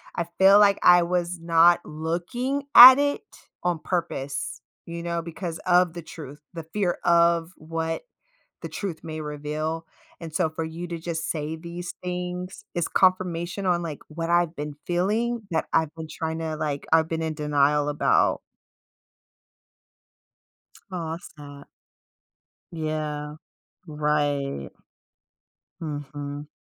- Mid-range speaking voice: Yes, medium, 165 Hz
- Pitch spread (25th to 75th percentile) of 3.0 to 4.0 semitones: No, narrow, 2.5 semitones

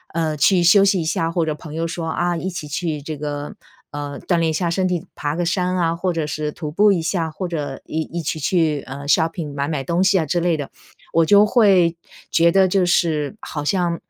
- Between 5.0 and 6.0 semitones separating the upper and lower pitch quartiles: No, average, 2.8 semitones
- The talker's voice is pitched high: No, medium, 165 Hz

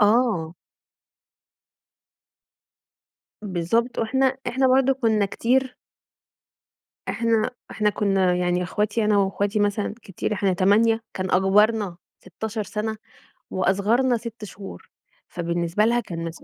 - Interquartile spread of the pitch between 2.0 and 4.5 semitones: Yes, average, 3.4 semitones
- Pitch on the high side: Yes, high, 210 Hz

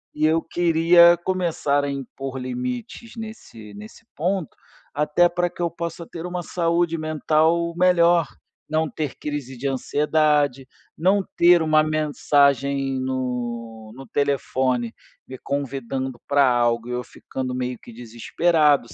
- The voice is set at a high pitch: No, medium, 145 Hz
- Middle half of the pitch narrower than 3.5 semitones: No, average, 4.6 semitones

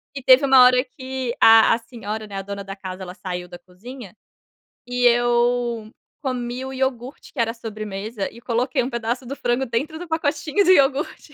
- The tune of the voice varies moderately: Yes, average, 3.4 semitones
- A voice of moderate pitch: No, high, 240 Hz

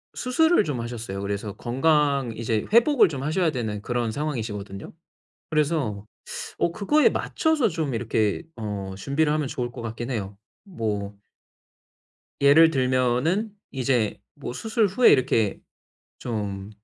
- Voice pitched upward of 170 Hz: No, low, 125 Hz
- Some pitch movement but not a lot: No, wide, 6.5 semitones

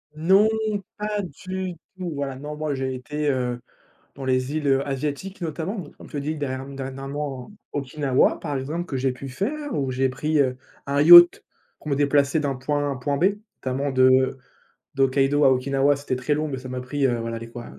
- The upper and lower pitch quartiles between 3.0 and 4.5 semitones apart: No, narrow, 2.5 semitones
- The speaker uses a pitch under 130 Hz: No, medium, 140 Hz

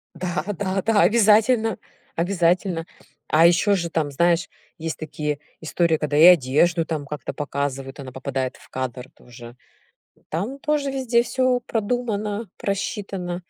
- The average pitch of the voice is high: No, medium, 175 Hz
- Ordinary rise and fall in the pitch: No, wide, 5.9 semitones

